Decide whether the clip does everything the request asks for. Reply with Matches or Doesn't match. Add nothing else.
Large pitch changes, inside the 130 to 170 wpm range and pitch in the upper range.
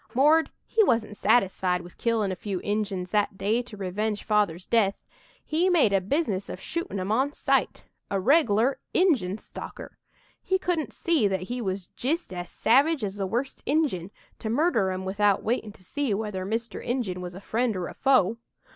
Doesn't match